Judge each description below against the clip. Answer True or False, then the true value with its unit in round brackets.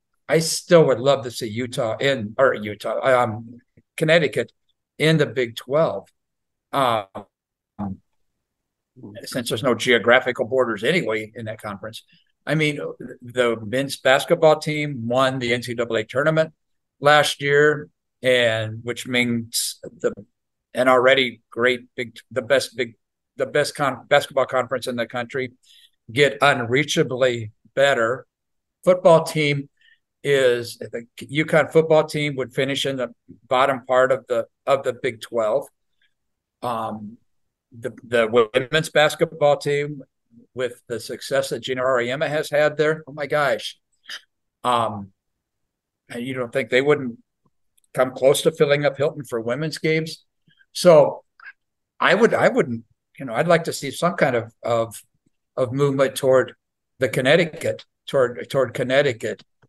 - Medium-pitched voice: False (130 Hz)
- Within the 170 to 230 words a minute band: False (135 wpm)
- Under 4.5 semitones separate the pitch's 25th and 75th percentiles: True (3.6 semitones)